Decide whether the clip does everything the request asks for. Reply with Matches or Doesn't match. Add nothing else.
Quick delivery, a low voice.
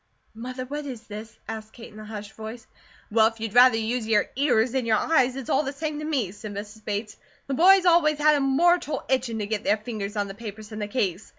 Doesn't match